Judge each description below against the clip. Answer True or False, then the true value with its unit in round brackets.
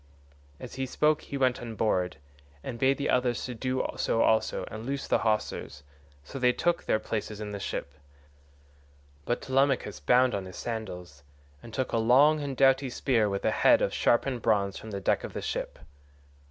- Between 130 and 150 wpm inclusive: False (185 wpm)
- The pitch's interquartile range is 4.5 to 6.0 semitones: False (3.8 semitones)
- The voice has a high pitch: False (120 Hz)